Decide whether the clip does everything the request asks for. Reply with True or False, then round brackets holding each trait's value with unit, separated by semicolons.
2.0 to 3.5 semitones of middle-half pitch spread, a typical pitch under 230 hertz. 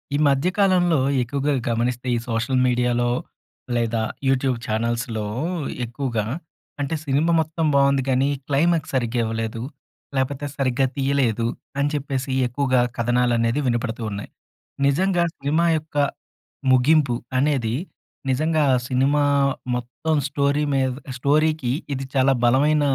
True (3.2 semitones; 135 Hz)